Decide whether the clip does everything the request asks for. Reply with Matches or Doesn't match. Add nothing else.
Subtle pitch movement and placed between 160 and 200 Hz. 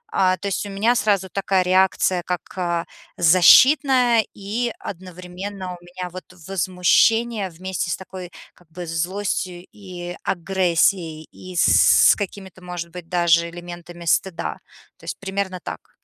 Matches